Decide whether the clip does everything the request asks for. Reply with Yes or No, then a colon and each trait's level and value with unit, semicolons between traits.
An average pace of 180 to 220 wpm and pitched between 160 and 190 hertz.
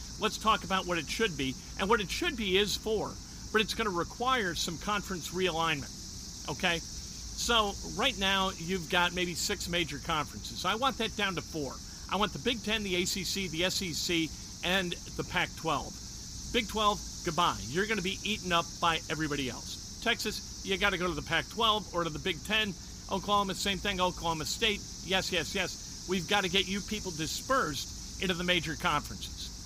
Yes: average, 190 wpm; medium, 185 Hz